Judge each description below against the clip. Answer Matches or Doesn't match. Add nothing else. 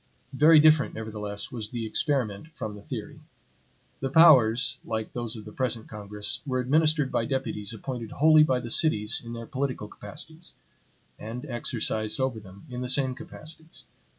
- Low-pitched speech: Matches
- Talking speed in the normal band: Matches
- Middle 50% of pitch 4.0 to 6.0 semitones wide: Matches